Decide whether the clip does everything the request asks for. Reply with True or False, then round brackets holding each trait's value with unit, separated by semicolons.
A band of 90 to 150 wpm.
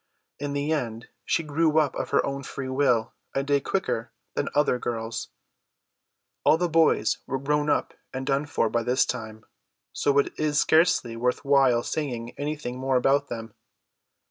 False (170 wpm)